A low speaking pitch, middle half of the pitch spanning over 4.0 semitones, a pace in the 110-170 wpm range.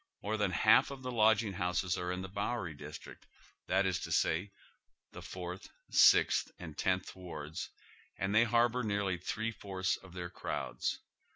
No: very low, 95 Hz; average, 3.2 semitones; average, 165 wpm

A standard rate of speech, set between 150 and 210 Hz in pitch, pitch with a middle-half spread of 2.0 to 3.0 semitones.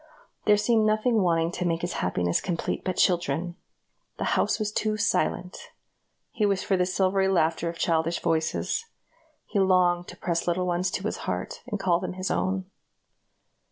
Yes: average, 170 wpm; medium, 185 Hz; narrow, 2.5 semitones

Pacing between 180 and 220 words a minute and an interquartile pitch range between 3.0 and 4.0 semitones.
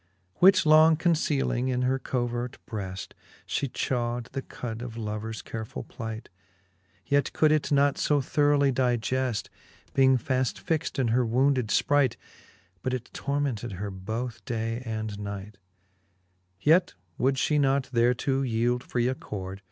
No: average, 145 wpm; average, 3.6 semitones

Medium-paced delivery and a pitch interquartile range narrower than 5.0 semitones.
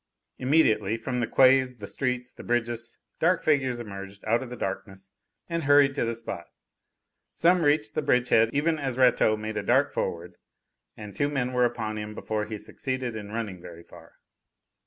Yes: average, 180 wpm; average, 3.7 semitones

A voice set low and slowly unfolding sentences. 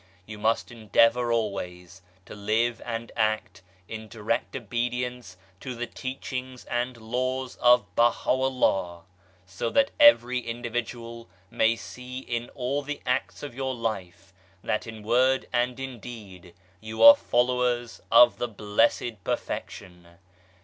Yes: low, 120 Hz; slow, 130 wpm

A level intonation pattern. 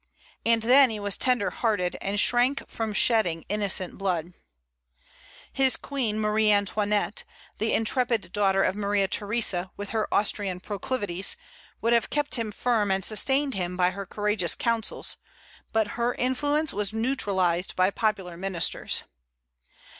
No: average, 3.3 semitones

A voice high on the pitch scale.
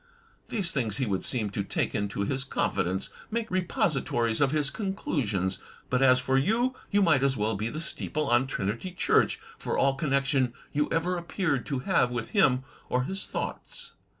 No: low, 135 Hz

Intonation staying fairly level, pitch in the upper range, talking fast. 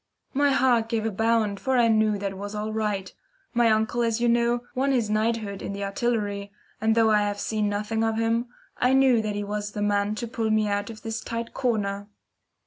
Yes: narrow, 2.1 semitones; high, 220 Hz; fast, 220 wpm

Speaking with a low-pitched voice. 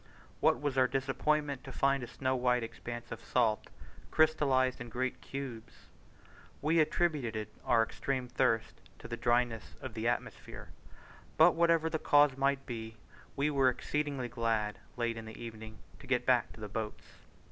Yes: low, 125 Hz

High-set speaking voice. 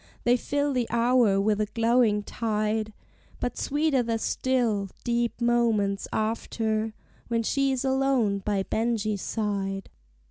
Yes: high, 225 Hz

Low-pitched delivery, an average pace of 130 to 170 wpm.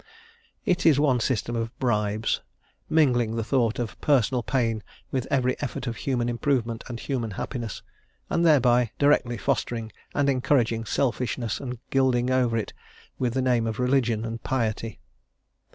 Yes: low, 120 Hz; average, 150 wpm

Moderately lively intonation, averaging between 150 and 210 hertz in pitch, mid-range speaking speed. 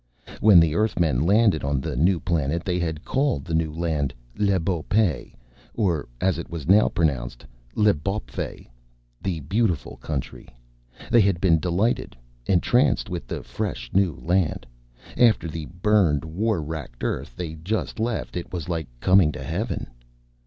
No: average, 4.3 semitones; very low, 85 Hz; average, 155 wpm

